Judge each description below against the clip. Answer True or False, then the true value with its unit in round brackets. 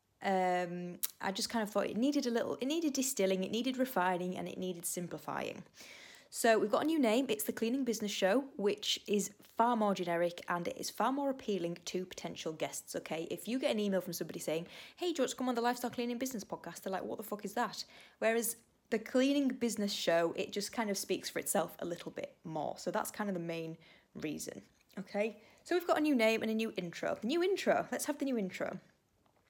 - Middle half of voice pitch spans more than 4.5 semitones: True (5.1 semitones)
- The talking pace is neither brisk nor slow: False (225 wpm)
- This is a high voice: True (215 Hz)